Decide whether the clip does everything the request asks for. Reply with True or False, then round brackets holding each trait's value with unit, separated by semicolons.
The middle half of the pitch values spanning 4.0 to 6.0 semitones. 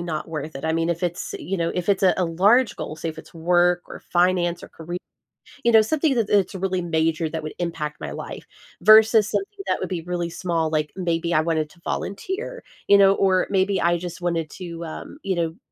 False (2.8 semitones)